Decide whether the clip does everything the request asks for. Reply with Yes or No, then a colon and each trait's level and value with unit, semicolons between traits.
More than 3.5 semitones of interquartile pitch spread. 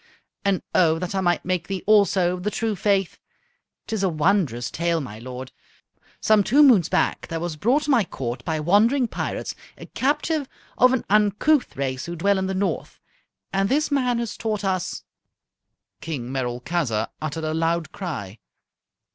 Yes: average, 5.3 semitones